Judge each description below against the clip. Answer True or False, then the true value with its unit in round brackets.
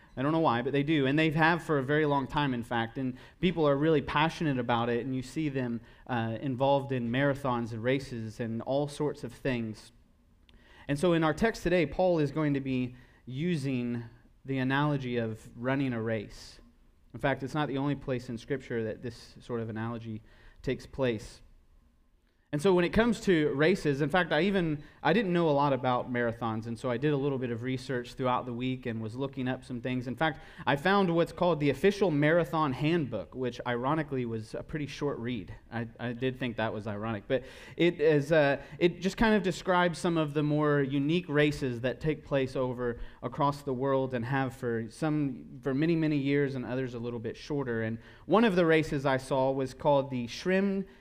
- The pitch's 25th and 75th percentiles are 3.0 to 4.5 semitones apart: True (4.1 semitones)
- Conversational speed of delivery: False (210 wpm)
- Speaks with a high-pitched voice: False (135 Hz)